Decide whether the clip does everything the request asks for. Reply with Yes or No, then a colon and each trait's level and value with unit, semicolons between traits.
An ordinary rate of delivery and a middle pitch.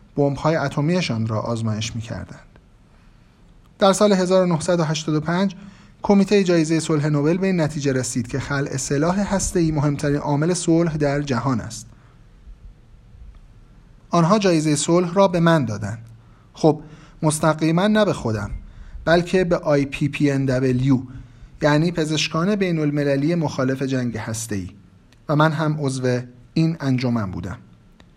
Yes: average, 120 wpm; medium, 145 Hz